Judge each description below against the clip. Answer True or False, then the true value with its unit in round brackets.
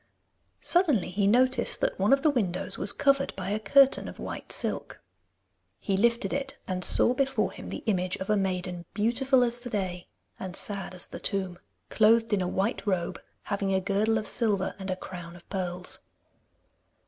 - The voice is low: False (200 Hz)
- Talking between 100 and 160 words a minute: False (185 wpm)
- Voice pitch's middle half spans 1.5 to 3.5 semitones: False (4.7 semitones)